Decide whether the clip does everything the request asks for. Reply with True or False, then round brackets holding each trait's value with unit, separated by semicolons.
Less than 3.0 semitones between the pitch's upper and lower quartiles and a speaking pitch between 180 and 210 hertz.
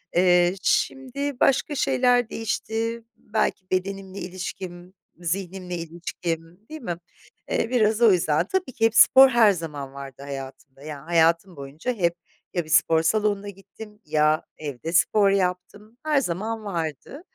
False (5.2 semitones; 185 Hz)